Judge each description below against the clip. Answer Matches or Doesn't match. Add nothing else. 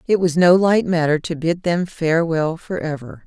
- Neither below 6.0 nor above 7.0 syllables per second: Doesn't match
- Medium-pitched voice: Matches